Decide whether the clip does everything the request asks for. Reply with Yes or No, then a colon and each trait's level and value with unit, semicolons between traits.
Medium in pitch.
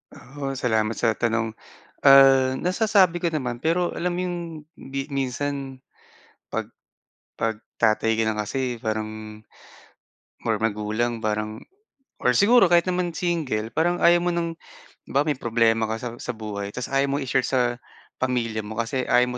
No: low, 125 Hz